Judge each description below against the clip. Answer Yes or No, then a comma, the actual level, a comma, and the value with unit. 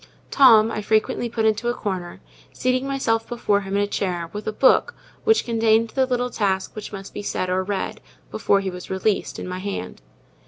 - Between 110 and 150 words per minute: No, average, 200 wpm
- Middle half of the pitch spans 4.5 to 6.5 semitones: No, average, 3.6 semitones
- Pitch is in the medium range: No, high, 215 Hz